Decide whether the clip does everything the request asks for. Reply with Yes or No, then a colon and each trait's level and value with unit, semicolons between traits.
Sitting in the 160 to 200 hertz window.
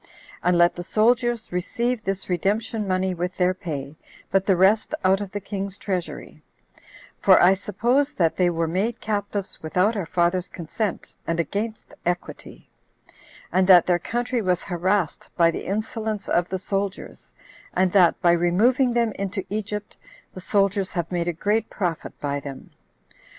Yes: high, 190 Hz